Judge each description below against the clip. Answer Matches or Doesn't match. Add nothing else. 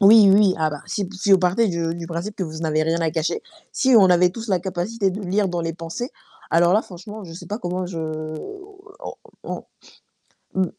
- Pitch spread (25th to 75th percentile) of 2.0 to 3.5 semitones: Doesn't match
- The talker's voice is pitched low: Doesn't match